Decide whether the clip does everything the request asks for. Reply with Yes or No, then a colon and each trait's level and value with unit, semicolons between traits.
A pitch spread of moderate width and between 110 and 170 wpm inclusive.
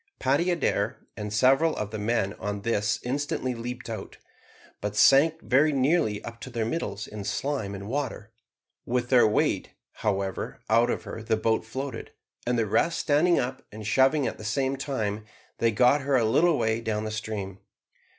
No: average, 4.1 semitones; average, 180 wpm